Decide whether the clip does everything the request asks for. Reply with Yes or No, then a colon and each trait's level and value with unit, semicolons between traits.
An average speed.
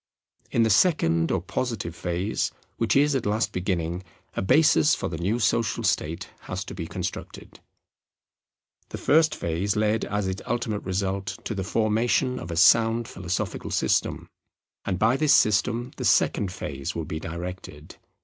Yes: average, 160 wpm